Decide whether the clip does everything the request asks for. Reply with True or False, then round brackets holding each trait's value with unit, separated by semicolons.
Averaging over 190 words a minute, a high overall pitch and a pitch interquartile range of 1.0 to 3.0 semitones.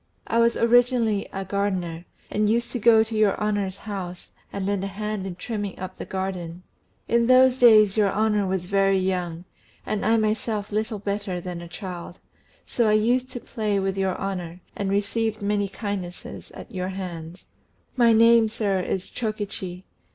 False (175 wpm; 200 Hz; 2.7 semitones)